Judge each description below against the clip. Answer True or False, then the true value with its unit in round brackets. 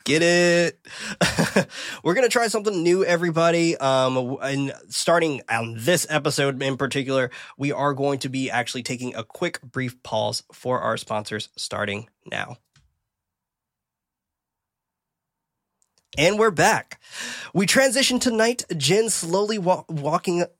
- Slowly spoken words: True (125 wpm)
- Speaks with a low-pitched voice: False (150 Hz)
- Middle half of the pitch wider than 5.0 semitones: True (5.5 semitones)